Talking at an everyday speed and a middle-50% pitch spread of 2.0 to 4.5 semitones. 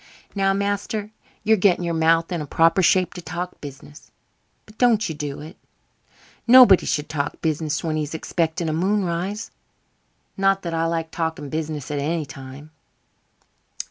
Yes: average, 155 wpm; average, 3.9 semitones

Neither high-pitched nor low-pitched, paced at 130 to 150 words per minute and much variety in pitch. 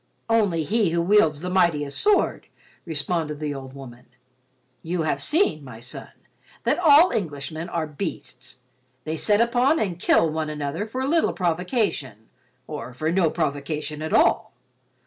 Yes: medium, 160 Hz; average, 145 wpm; wide, 5.7 semitones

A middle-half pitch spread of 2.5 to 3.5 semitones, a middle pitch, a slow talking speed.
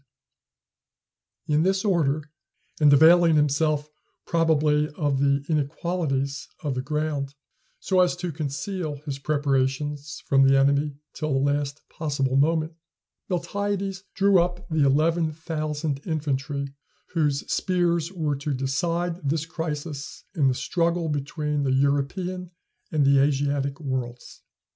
Yes: average, 3.1 semitones; medium, 150 Hz; slow, 125 wpm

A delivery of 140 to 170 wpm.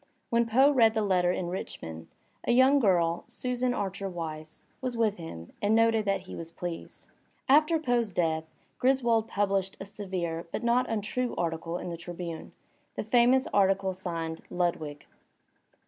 Yes: average, 165 wpm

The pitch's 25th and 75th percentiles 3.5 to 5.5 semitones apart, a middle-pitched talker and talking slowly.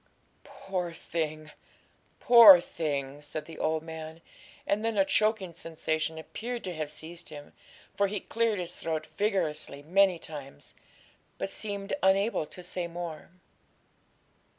Yes: average, 4.0 semitones; medium, 170 Hz; slow, 130 wpm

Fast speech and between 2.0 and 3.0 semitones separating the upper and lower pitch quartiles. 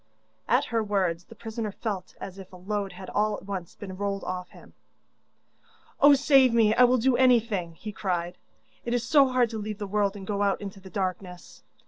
No: fast, 210 wpm; average, 3.5 semitones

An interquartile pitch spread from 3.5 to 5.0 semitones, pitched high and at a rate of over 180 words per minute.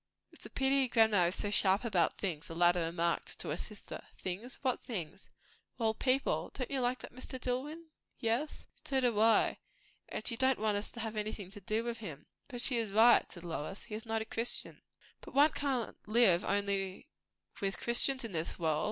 Yes: average, 4.5 semitones; high, 220 Hz; fast, 205 wpm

